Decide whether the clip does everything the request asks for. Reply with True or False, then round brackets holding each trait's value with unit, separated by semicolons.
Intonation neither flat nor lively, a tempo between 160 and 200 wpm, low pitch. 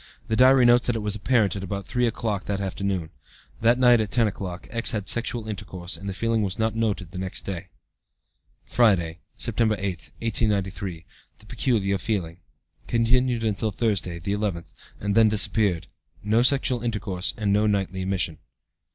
True (3.1 semitones; 170 wpm; 105 Hz)